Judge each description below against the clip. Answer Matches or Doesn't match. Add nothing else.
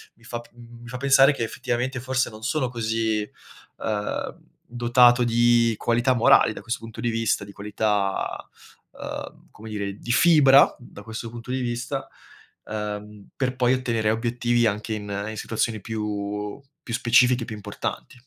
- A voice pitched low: Matches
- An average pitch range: Doesn't match